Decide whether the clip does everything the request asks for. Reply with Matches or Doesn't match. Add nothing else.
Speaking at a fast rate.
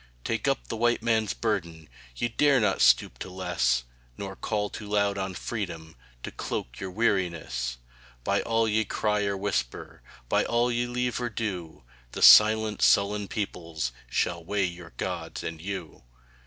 Doesn't match